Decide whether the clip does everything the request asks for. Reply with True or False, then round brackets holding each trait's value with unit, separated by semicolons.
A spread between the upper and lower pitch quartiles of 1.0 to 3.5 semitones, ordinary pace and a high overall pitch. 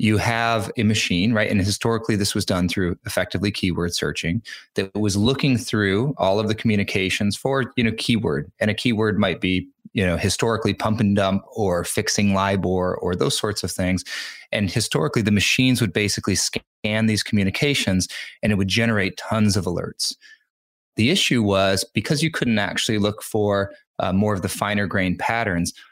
False (2.8 semitones; 180 wpm; 105 Hz)